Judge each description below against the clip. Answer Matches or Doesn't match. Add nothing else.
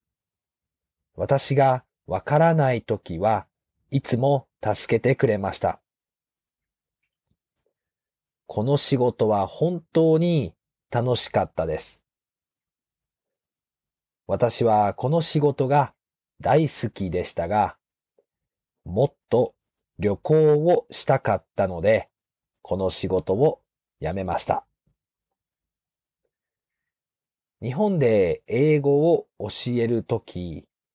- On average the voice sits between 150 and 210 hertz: Doesn't match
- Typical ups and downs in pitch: Doesn't match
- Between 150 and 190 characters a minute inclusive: Matches